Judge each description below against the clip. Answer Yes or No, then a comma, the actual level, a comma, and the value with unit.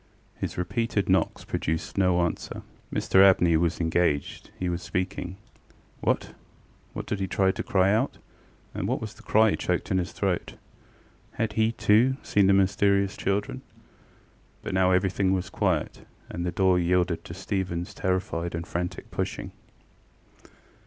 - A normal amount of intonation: No, narrow, 2.0 semitones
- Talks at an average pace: Yes, average, 150 wpm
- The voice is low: Yes, very low, 95 Hz